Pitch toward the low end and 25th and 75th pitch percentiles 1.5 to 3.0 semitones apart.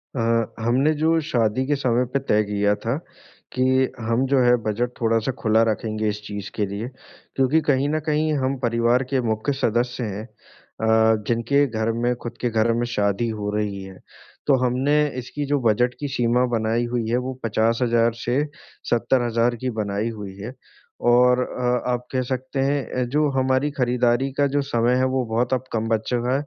Yes: low, 120 Hz; average, 2.7 semitones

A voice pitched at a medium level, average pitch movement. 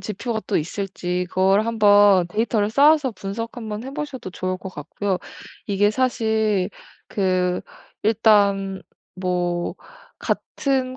No: high, 205 Hz; average, 3.5 semitones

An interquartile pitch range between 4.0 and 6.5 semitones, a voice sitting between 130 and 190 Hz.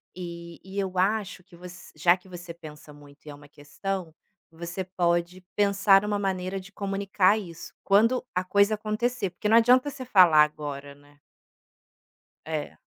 No: average, 3.2 semitones; medium, 185 Hz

